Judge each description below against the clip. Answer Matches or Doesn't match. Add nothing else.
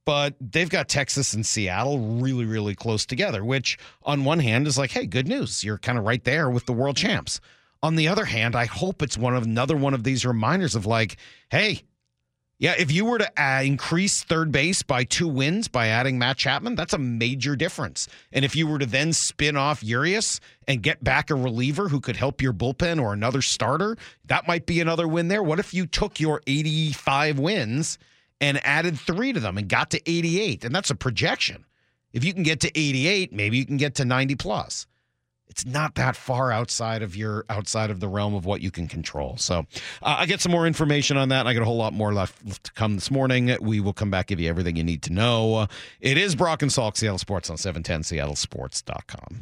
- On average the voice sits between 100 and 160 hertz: Matches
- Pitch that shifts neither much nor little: Doesn't match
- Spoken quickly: Matches